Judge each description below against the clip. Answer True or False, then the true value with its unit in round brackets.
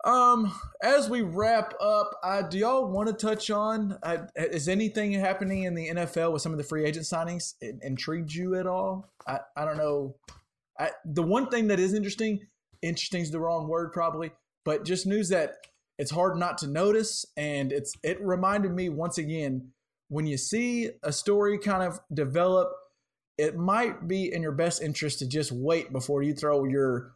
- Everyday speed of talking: True (190 wpm)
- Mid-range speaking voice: True (175 Hz)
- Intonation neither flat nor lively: True (5.0 semitones)